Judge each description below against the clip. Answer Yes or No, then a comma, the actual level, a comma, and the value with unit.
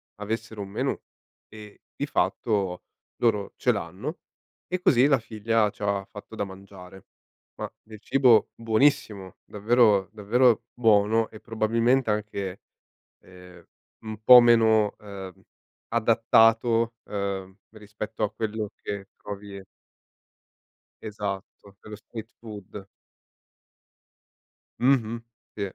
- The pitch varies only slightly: Yes, narrow, 2.2 semitones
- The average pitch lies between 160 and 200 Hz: No, low, 105 Hz